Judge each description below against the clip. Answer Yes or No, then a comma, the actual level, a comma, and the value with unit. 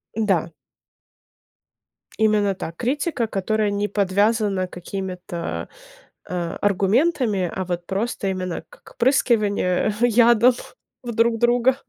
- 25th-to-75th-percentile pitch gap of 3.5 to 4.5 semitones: Yes, average, 4.0 semitones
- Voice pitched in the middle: No, high, 205 Hz